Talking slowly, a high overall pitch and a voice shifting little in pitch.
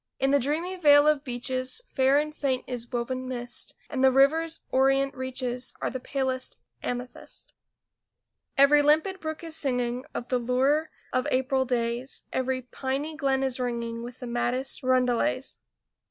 No: average, 155 wpm; very high, 260 Hz; narrow, 2.3 semitones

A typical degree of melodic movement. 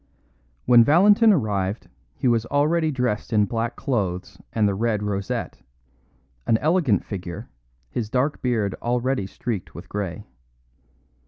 Yes: average, 4.6 semitones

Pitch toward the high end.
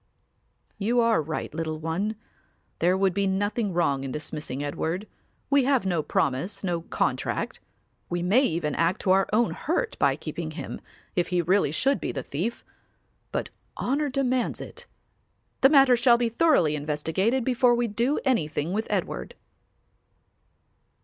Yes: high, 195 Hz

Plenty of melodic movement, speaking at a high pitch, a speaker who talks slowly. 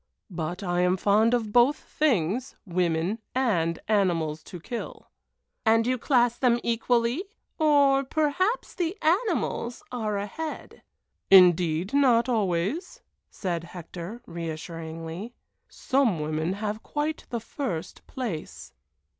Yes: wide, 6.9 semitones; high, 220 Hz; slow, 115 wpm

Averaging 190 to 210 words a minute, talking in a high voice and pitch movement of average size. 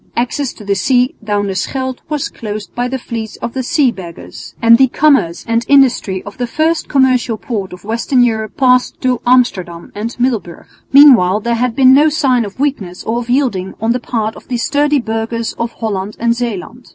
Yes: average, 200 wpm; high, 235 Hz; average, 3.5 semitones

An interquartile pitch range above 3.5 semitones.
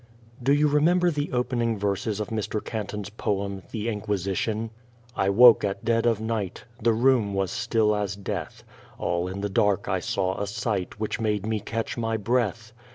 No: narrow, 2.6 semitones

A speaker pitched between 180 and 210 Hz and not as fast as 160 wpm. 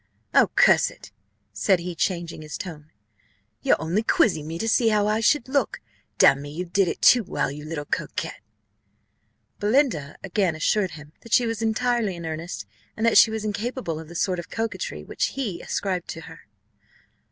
No: medium, 185 Hz; average, 185 wpm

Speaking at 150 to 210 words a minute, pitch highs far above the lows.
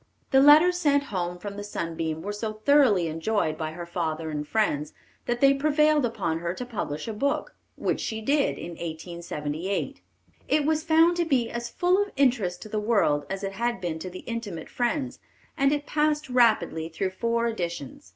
Yes: average, 190 wpm; wide, 8.4 semitones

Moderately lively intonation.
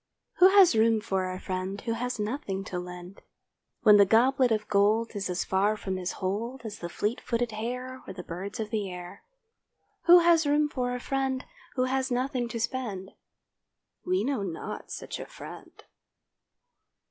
Yes: average, 5.0 semitones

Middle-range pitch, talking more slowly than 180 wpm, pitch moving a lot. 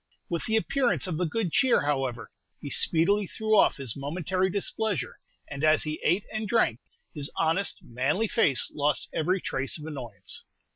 Yes: medium, 160 Hz; average, 165 wpm; wide, 6.1 semitones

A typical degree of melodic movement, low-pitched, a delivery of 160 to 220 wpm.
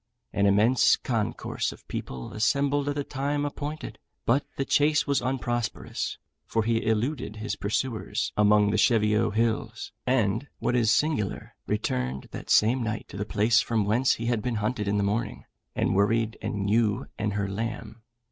Yes: average, 3.3 semitones; low, 110 Hz; average, 165 wpm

